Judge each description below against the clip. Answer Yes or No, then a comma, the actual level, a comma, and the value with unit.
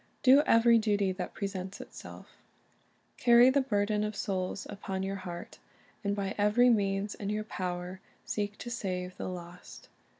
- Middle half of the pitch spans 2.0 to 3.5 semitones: Yes, narrow, 2.4 semitones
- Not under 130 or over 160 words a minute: Yes, average, 155 wpm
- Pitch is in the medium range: No, high, 200 Hz